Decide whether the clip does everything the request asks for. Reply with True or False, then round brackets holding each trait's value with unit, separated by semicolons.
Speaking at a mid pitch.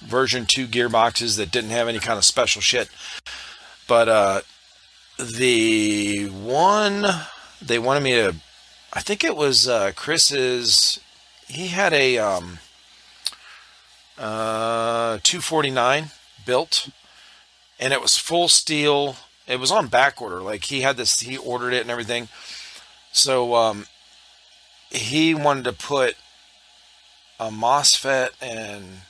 False (120 Hz)